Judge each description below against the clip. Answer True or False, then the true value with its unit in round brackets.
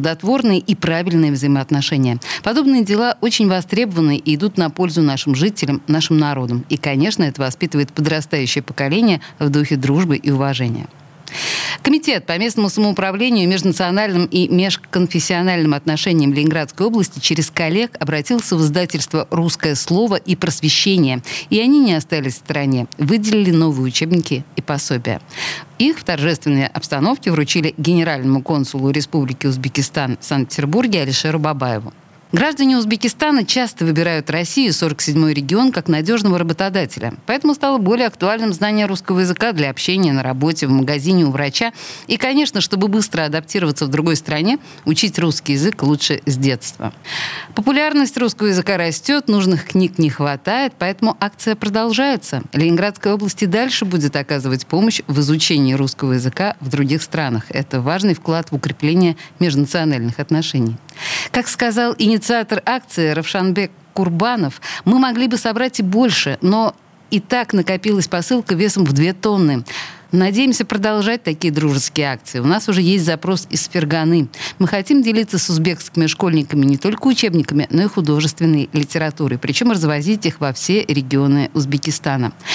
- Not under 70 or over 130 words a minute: False (140 wpm)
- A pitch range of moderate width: False (5.8 semitones)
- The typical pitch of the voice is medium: True (165 Hz)